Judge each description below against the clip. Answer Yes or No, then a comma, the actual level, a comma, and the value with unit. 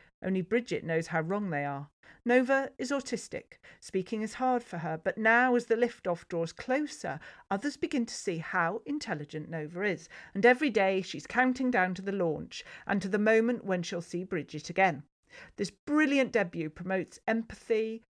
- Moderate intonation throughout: No, wide, 5.7 semitones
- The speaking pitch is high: Yes, high, 200 Hz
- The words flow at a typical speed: Yes, average, 175 wpm